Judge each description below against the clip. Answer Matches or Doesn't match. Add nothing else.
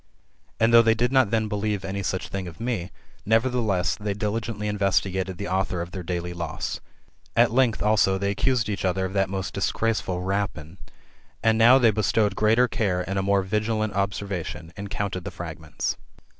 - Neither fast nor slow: Matches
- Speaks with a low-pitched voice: Matches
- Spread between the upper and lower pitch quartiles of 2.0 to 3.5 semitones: Matches